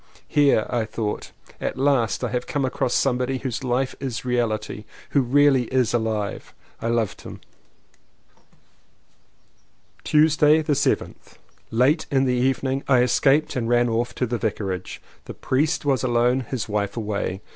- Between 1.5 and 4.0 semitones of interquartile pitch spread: Yes, average, 2.9 semitones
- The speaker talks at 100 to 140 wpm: No, average, 155 wpm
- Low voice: Yes, low, 125 Hz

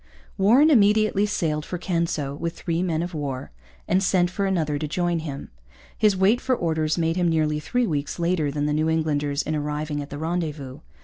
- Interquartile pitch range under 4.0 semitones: Yes, average, 3.6 semitones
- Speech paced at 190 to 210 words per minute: Yes, average, 195 wpm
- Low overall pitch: No, medium, 165 Hz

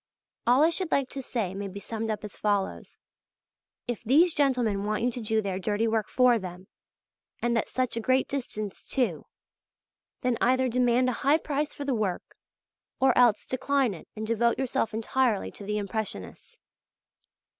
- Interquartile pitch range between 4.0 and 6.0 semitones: No, average, 3.5 semitones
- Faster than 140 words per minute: Yes, average, 175 wpm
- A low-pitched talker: No, high, 235 Hz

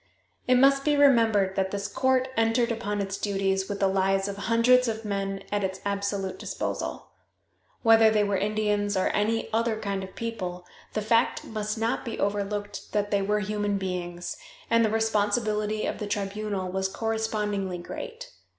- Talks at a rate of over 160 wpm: Yes, average, 170 wpm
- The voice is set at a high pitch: Yes, high, 205 Hz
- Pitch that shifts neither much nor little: No, narrow, 2.3 semitones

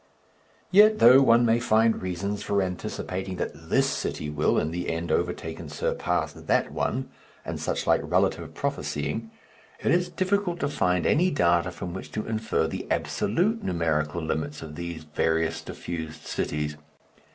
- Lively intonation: Yes, wide, 6.4 semitones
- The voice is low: Yes, very low, 90 Hz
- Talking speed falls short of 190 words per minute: Yes, average, 155 wpm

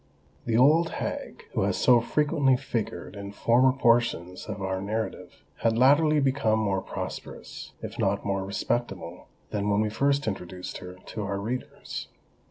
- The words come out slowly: No, average, 155 wpm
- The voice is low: Yes, low, 110 Hz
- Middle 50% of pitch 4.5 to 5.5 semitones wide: Yes, average, 4.9 semitones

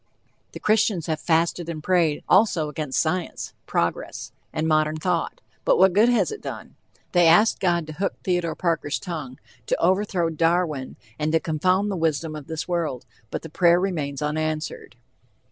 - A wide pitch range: No, average, 2.7 semitones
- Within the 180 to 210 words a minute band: No, average, 165 wpm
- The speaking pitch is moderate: Yes, medium, 165 Hz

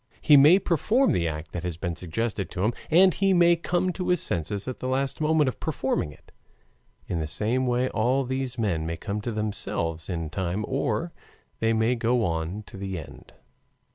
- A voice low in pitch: Yes, low, 115 Hz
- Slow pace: No, average, 195 wpm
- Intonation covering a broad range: Yes, wide, 7.7 semitones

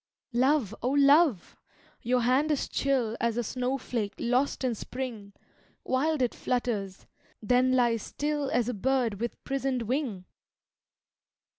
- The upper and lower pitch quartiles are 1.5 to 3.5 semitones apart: Yes, average, 2.8 semitones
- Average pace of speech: No, slow, 130 wpm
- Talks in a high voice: Yes, very high, 250 Hz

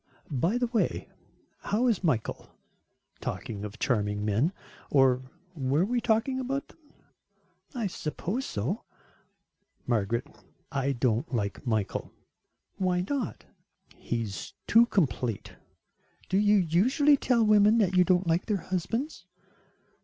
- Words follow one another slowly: Yes, slow, 125 wpm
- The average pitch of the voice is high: No, medium, 180 Hz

